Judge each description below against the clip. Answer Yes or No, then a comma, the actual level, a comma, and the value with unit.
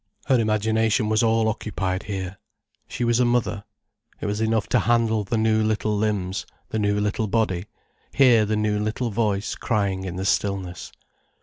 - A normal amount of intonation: No, narrow, 1.9 semitones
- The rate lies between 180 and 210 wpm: No, average, 170 wpm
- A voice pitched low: Yes, low, 110 Hz